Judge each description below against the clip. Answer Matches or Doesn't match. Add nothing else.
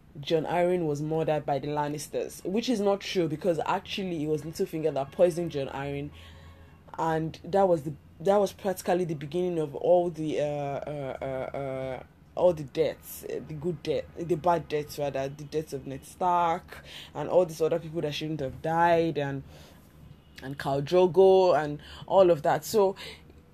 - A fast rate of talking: Doesn't match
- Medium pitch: Matches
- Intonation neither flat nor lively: Matches